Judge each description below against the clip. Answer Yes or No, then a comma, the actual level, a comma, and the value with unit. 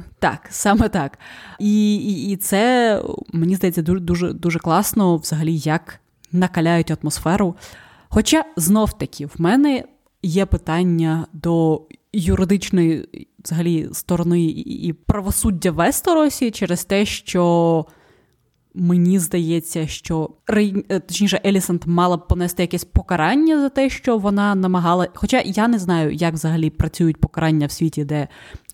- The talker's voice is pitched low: No, medium, 175 Hz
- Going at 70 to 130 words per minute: Yes, average, 125 wpm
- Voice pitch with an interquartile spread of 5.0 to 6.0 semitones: No, average, 3.7 semitones